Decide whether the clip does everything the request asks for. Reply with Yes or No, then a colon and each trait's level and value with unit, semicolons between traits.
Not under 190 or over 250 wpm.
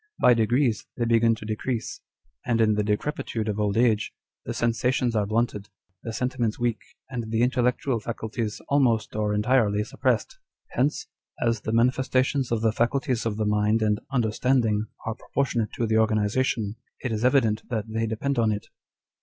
No: average, 165 wpm